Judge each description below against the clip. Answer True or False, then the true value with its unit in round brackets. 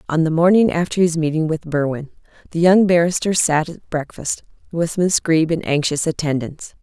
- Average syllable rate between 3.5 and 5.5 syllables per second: True (5.2 syllables/s)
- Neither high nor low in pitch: True (165 Hz)